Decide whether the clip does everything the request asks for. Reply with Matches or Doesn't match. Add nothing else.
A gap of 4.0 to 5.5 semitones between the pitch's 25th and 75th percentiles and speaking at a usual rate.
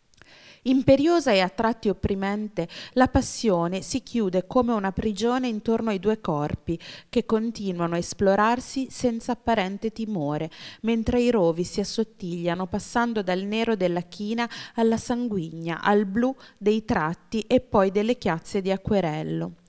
Matches